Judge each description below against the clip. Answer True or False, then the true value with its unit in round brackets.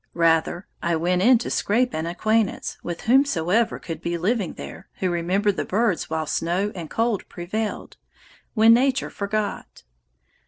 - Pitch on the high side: True (195 Hz)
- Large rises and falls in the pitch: False (4.7 semitones)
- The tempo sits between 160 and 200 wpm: False (150 wpm)